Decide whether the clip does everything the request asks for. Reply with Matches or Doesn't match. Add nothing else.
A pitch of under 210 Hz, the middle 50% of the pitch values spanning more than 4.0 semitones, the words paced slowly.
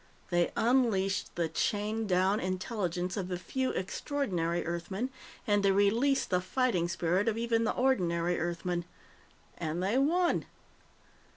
Matches